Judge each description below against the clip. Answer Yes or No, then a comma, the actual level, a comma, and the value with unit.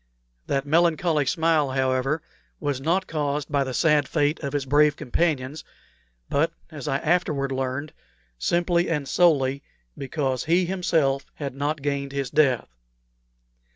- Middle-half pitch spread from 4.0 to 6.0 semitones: No, average, 2.8 semitones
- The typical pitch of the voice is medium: Yes, medium, 145 Hz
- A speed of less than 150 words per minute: Yes, slow, 135 wpm